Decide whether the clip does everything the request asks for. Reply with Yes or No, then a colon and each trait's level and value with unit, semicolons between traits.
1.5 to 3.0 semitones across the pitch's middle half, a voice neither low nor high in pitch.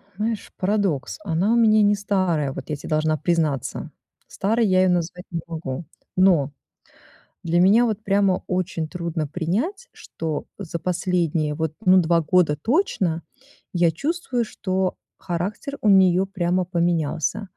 No: average, 3.7 semitones; medium, 180 Hz